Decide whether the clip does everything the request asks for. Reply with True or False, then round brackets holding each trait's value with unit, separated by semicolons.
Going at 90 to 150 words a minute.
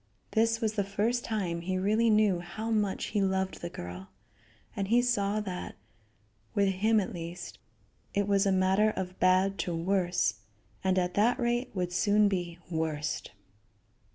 False (160 wpm)